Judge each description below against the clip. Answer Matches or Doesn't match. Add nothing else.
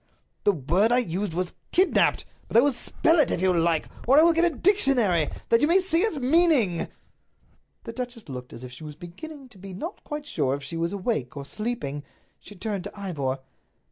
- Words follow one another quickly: Matches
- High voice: Matches